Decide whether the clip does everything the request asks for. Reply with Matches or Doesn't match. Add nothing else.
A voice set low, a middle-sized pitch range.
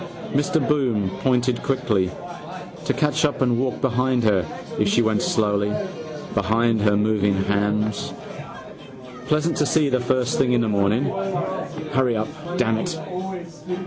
Matches